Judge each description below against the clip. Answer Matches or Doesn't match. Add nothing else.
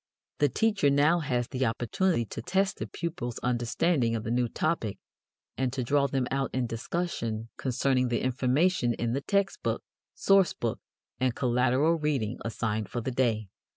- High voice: Doesn't match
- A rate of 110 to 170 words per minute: Matches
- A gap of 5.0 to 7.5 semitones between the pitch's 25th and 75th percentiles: Doesn't match